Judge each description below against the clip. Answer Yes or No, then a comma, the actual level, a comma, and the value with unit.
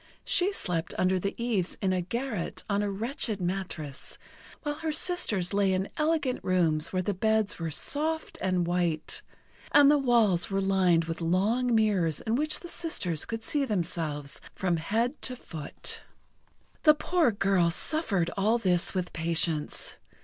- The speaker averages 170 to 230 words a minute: No, average, 155 wpm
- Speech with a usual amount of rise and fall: No, wide, 5.9 semitones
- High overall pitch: Yes, high, 195 Hz